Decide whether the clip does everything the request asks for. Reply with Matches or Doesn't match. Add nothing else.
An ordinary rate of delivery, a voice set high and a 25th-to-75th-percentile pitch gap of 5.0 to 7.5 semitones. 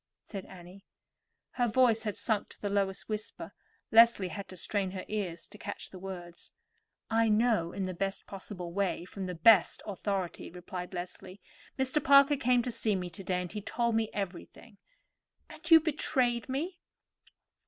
Doesn't match